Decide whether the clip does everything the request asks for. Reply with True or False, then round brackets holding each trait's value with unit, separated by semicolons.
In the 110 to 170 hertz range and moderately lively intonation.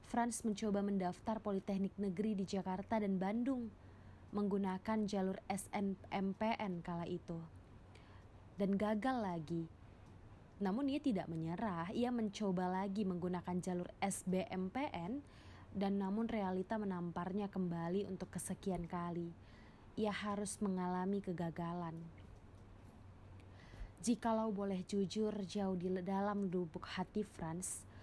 False (190 Hz; 3.2 semitones)